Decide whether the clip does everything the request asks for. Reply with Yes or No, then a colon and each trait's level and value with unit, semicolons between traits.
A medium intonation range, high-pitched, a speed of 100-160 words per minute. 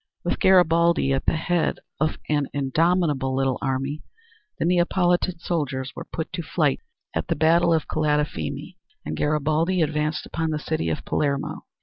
No: average, 3.3 semitones; medium, 155 Hz; average, 150 wpm